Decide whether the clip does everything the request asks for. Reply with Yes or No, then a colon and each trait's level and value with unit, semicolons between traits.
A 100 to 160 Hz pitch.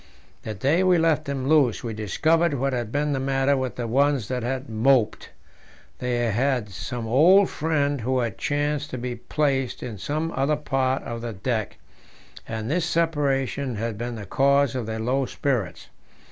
Yes: low, 135 Hz